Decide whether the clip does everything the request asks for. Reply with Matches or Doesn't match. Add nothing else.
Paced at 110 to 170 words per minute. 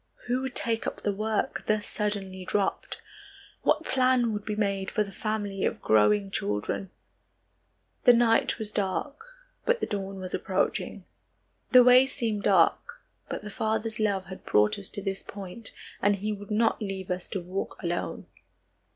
Matches